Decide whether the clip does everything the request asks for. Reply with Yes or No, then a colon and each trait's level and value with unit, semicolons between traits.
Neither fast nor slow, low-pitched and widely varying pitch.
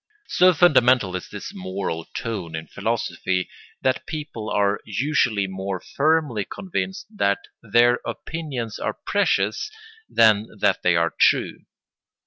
No: slow, 120 wpm; low, 110 Hz; wide, 6.7 semitones